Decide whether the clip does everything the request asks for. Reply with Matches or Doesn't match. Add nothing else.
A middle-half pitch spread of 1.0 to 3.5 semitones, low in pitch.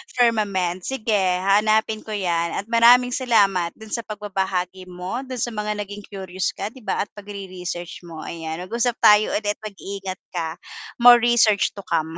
Doesn't match